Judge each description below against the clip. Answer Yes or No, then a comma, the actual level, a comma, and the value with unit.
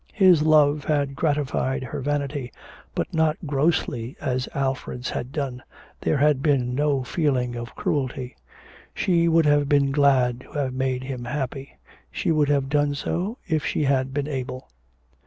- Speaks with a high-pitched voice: No, medium, 140 Hz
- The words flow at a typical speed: Yes, average, 155 wpm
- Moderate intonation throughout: No, narrow, 2.3 semitones